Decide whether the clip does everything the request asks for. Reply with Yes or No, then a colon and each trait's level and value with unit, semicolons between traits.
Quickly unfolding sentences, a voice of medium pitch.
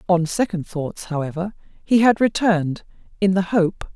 No: average, 150 wpm; medium, 180 Hz